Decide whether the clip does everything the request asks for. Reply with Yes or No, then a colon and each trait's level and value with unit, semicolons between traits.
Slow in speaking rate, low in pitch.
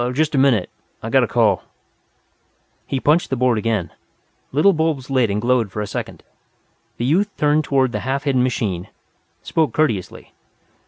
No: average, 165 wpm; low, 130 Hz